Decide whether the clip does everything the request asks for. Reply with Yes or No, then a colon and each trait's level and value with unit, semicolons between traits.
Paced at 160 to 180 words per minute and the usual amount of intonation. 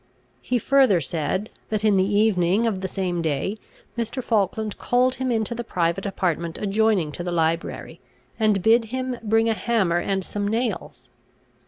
Yes: average, 165 wpm; average, 4.1 semitones